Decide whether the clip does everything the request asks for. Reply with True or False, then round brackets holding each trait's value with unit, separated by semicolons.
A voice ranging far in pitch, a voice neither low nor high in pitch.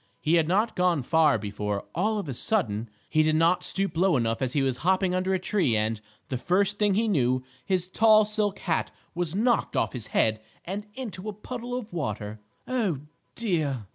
True (7.9 semitones; 175 Hz)